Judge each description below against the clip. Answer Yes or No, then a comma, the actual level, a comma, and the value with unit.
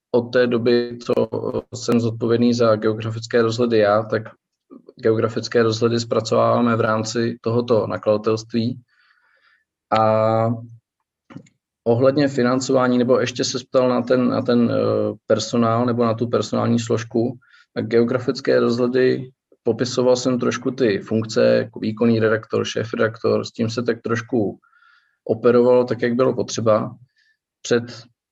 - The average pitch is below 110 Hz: No, low, 120 Hz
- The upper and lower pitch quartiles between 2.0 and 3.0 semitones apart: No, narrow, 1.6 semitones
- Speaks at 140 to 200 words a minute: No, average, 125 wpm